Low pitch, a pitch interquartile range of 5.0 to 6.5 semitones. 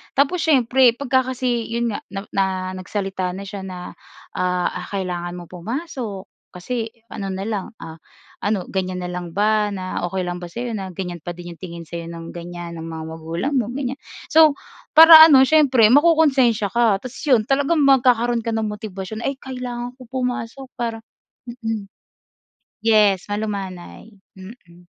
No: high, 215 Hz; wide, 5.5 semitones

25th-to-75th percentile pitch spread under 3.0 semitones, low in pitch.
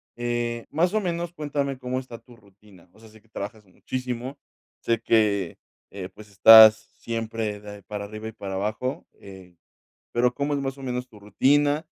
No: average, 3.8 semitones; low, 115 Hz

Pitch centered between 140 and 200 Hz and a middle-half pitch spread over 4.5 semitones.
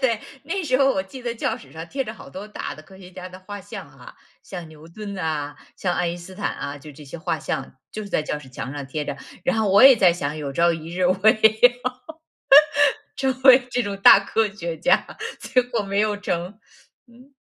Yes: high, 190 Hz; wide, 5.4 semitones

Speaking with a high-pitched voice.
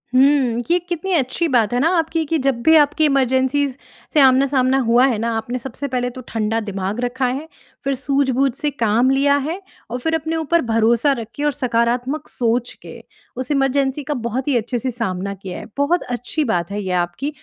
Yes: very high, 260 Hz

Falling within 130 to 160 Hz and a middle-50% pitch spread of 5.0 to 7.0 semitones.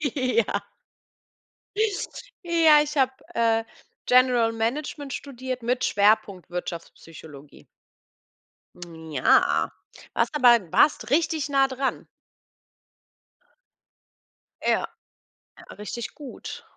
No: high, 245 Hz; average, 5.3 semitones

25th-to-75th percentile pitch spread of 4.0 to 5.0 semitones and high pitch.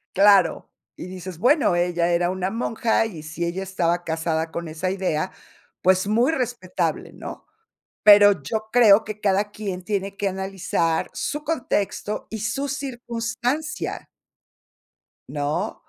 Yes: average, 4.3 semitones; high, 195 Hz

